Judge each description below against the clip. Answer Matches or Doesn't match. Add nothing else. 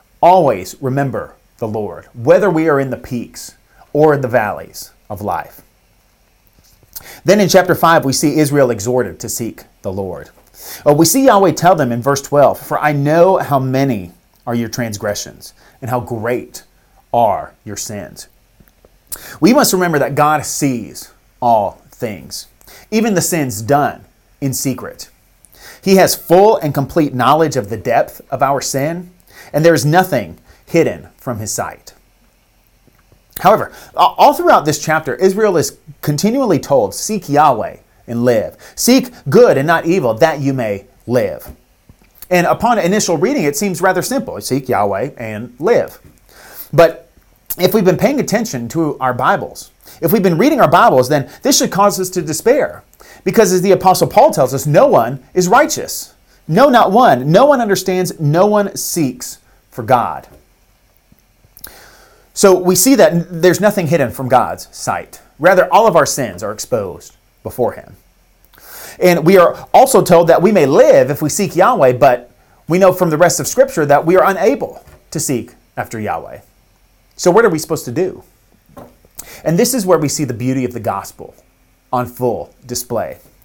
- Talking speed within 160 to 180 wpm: Matches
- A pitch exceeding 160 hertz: Doesn't match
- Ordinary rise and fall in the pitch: Doesn't match